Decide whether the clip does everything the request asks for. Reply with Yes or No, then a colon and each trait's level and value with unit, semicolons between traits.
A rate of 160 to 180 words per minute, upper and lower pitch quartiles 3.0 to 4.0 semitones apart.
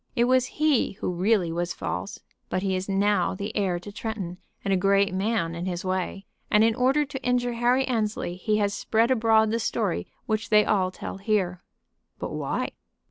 No: average, 190 wpm; average, 3.6 semitones